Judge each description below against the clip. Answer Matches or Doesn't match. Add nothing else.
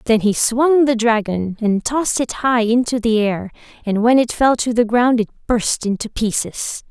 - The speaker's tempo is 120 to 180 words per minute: Doesn't match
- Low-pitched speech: Doesn't match